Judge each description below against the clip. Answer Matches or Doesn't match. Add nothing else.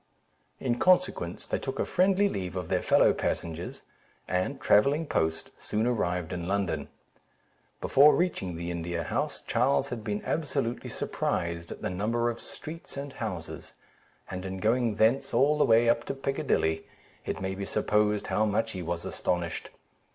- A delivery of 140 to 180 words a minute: Matches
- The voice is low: Matches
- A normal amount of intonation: Doesn't match